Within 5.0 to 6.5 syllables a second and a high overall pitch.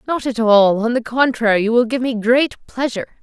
Yes: 5.7 syllables/s; high, 235 Hz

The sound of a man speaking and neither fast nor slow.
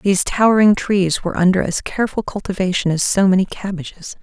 No: female; average, 170 wpm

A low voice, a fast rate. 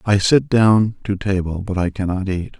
Yes: low, 100 Hz; fast, 210 wpm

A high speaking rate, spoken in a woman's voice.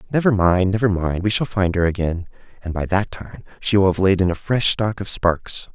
No: fast, 240 wpm; male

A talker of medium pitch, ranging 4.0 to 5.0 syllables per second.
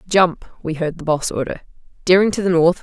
No: medium, 170 Hz; 5.6 syllables/s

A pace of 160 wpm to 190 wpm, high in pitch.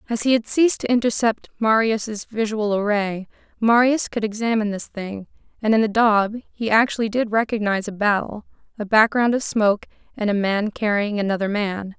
Yes: average, 170 wpm; high, 215 Hz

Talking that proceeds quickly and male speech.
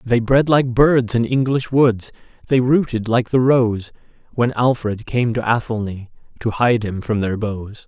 No: average, 175 wpm; male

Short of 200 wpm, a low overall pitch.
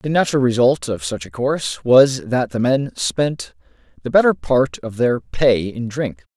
Yes: average, 190 wpm; low, 120 Hz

